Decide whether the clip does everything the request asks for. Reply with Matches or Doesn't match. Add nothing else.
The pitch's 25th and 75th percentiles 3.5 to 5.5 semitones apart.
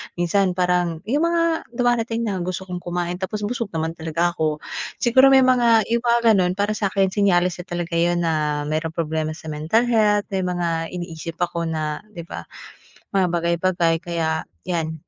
Matches